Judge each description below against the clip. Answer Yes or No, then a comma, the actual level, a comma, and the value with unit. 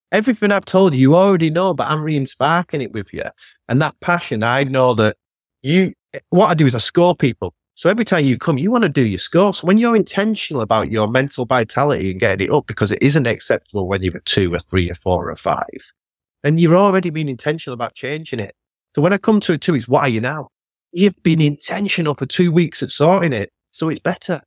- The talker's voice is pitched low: No, medium, 150 Hz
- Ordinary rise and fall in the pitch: No, wide, 6.6 semitones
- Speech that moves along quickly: Yes, fast, 240 wpm